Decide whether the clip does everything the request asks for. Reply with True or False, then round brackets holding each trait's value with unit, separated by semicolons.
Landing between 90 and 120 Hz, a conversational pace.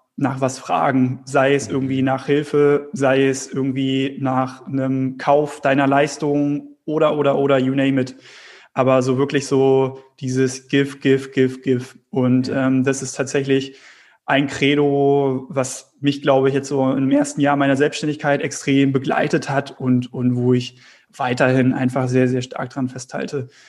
False (135 Hz; 160 wpm)